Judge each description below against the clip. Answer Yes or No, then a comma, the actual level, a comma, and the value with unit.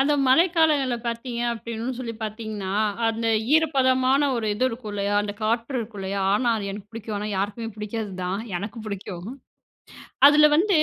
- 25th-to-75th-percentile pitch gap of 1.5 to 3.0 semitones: No, average, 4.0 semitones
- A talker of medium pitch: No, high, 230 Hz